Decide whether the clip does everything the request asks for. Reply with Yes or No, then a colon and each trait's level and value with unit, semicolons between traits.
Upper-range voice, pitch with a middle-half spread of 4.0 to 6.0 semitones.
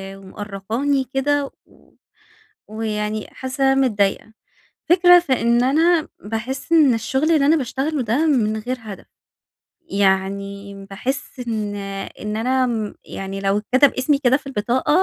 Yes: high, 240 Hz; average, 4.7 semitones